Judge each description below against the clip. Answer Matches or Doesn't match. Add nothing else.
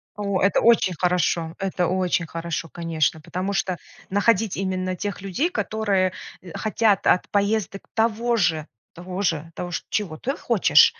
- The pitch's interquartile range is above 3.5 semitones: Doesn't match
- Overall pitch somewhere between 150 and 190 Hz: Matches